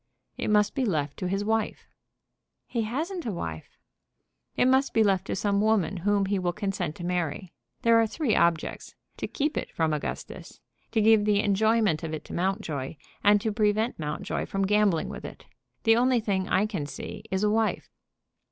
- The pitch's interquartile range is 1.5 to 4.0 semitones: Yes, average, 3.7 semitones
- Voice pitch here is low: No, high, 205 Hz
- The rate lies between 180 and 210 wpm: Yes, average, 190 wpm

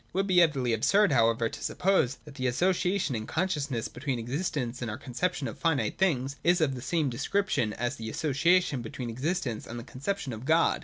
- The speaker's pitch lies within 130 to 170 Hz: Yes, medium, 140 Hz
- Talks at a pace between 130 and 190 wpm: No, average, 200 wpm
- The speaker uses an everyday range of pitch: No, wide, 6.5 semitones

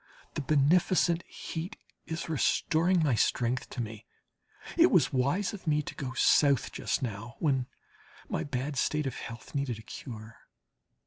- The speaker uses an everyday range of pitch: Yes, average, 4.7 semitones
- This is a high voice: No, medium, 140 Hz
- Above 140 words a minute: Yes, average, 150 wpm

